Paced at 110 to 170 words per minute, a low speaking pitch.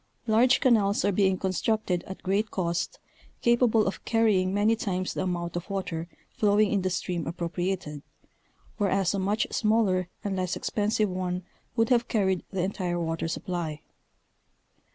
No: average, 150 wpm; high, 190 Hz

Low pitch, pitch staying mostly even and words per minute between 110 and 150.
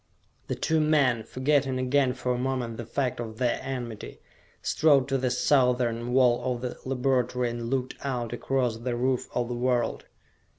No: low, 125 Hz; narrow, 1.7 semitones; average, 170 wpm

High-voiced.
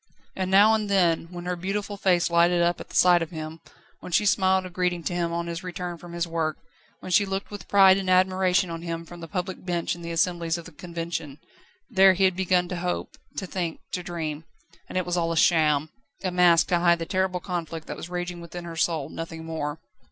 No: medium, 175 Hz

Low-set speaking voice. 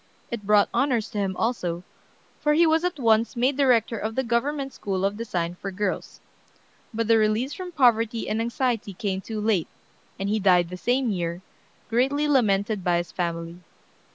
No: high, 220 Hz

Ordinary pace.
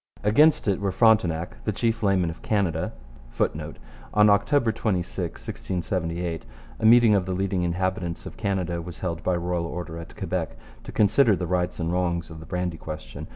Yes: average, 175 wpm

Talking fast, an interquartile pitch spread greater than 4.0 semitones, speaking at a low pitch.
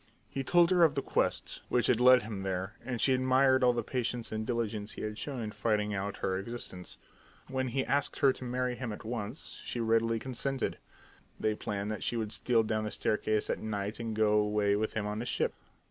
No: fast, 220 wpm; average, 3.2 semitones; low, 115 Hz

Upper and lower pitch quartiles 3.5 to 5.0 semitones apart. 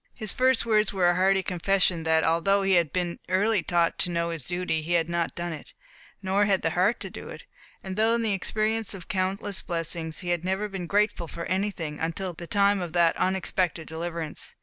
No: average, 2.7 semitones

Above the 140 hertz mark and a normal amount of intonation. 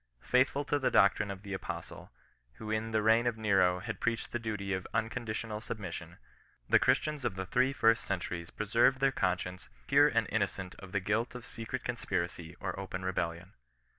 No: low, 105 Hz; average, 3.9 semitones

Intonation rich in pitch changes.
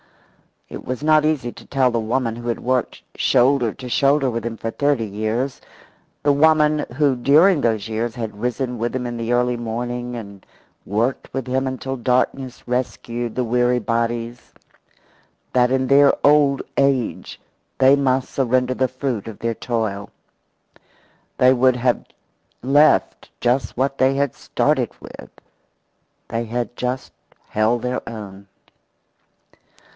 No: narrow, 2.4 semitones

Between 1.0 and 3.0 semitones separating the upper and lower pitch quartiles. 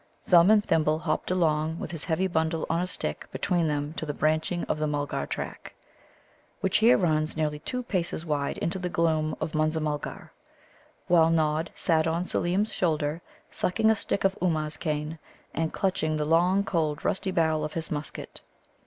Yes: narrow, 2.5 semitones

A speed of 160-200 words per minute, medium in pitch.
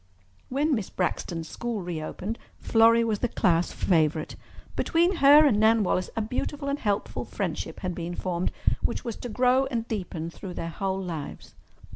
No: average, 165 wpm; high, 210 Hz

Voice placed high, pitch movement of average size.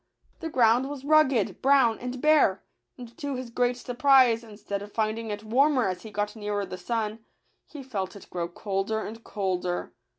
Yes: high, 225 Hz; average, 3.9 semitones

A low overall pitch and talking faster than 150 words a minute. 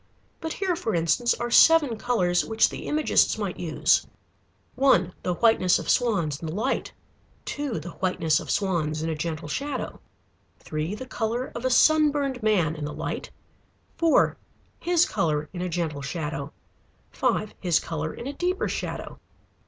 No: high, 200 Hz; average, 160 wpm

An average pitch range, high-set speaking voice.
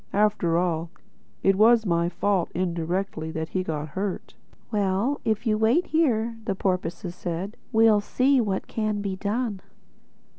Yes: average, 3.8 semitones; high, 200 Hz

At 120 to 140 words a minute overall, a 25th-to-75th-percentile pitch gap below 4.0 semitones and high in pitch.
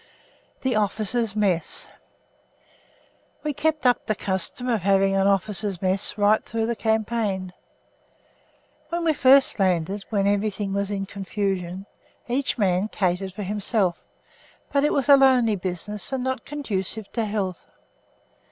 Yes: slow, 135 wpm; average, 3.6 semitones; high, 205 Hz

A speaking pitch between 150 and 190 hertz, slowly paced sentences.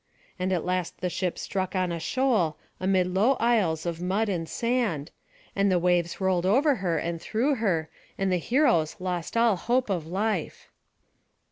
No: medium, 185 Hz; average, 170 wpm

